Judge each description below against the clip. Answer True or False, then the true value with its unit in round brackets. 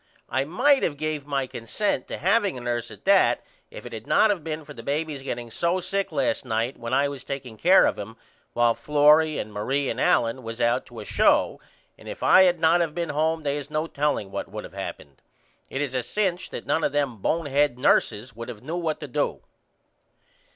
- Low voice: False (145 Hz)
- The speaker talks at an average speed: False (220 wpm)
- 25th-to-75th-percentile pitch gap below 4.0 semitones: False (5.1 semitones)